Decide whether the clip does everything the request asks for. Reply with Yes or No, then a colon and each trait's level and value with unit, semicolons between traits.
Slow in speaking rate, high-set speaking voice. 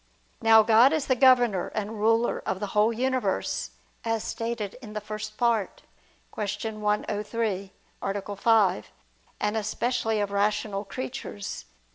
Yes: slow, 130 wpm; high, 215 Hz